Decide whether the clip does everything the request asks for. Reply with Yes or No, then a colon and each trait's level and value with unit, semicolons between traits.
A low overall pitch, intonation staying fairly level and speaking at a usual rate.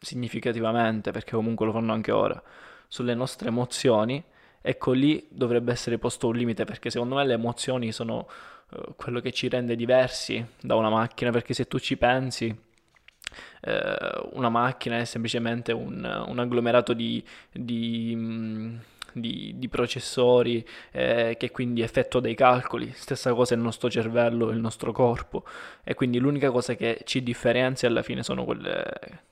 Yes: low, 120 Hz; narrow, 1.5 semitones; average, 150 wpm